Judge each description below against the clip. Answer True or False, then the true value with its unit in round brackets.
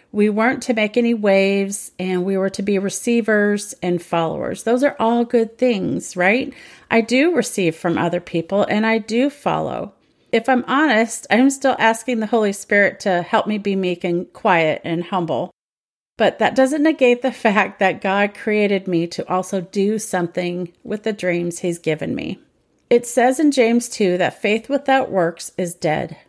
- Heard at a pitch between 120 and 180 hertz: False (210 Hz)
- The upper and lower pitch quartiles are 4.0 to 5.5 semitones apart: True (4.7 semitones)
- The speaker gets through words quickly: False (185 wpm)